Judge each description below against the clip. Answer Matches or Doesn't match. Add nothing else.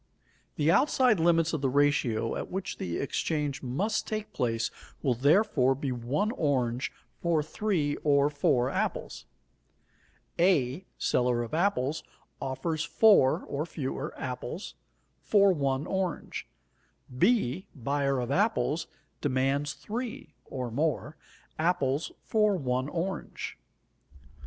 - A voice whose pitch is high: Doesn't match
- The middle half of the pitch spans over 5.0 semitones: Matches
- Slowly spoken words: Matches